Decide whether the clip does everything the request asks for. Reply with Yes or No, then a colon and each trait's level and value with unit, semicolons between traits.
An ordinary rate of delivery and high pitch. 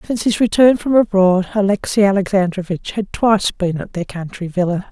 Yes: average, 170 wpm; high, 195 Hz